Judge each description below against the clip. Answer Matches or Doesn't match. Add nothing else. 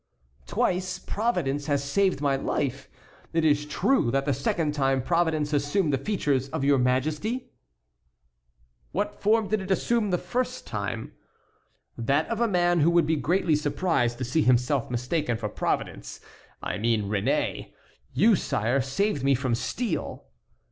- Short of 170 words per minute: Matches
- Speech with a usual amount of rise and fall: Doesn't match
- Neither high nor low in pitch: Matches